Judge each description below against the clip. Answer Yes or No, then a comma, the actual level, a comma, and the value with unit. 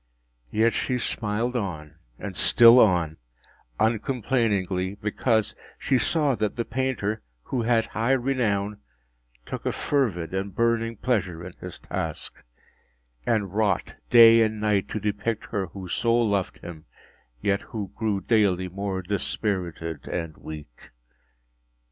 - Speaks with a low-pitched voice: Yes, low, 105 Hz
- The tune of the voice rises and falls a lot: No, average, 3.7 semitones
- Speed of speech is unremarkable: No, slow, 130 wpm